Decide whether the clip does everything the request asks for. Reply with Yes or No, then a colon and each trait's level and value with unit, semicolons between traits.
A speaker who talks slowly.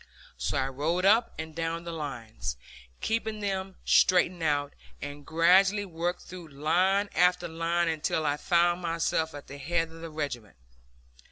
No: average, 155 wpm